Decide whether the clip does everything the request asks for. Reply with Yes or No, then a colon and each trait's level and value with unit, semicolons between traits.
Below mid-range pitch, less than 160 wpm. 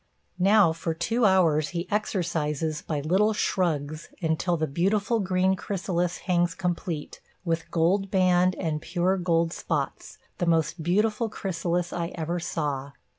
No: medium, 175 Hz; slow, 135 wpm